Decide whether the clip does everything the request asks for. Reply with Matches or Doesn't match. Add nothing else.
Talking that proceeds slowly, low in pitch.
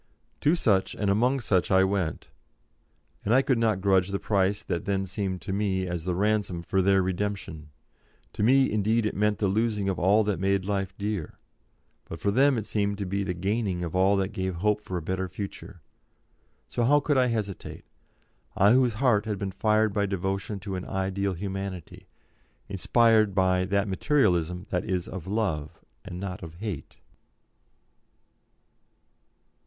Doesn't match